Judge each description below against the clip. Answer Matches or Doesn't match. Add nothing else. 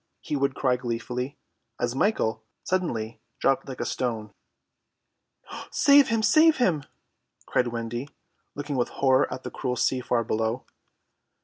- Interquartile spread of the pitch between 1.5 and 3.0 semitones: Doesn't match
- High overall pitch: Doesn't match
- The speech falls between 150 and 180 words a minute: Doesn't match